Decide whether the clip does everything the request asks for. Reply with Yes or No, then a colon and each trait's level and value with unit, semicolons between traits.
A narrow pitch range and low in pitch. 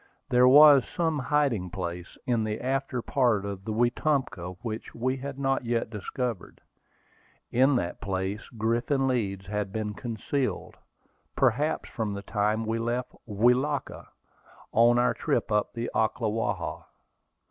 No: average, 3.7 semitones; low, 115 Hz